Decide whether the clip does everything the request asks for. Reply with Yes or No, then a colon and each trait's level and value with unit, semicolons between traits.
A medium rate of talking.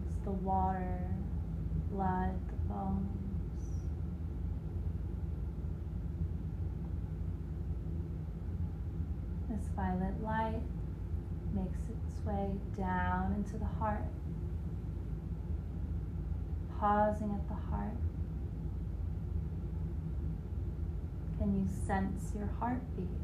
No: slow, 60 wpm